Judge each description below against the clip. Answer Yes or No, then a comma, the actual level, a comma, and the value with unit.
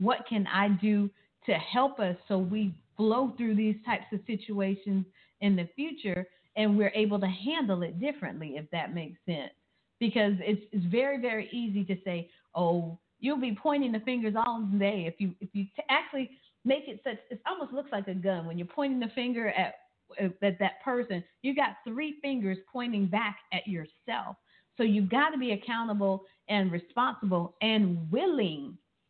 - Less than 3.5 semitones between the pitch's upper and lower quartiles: No, average, 4.3 semitones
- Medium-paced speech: Yes, average, 180 wpm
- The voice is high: Yes, high, 210 Hz